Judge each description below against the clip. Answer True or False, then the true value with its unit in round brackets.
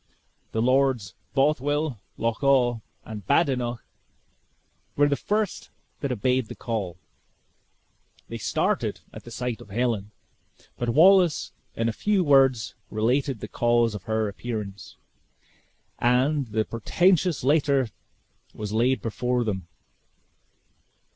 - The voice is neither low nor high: False (125 Hz)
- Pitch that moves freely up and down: False (3.9 semitones)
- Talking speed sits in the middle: False (115 wpm)